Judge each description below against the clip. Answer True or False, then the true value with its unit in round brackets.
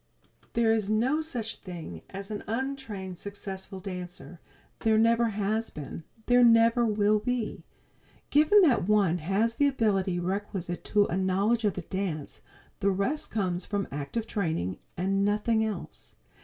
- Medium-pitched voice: False (205 Hz)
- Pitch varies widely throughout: False (3.4 semitones)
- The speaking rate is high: False (145 wpm)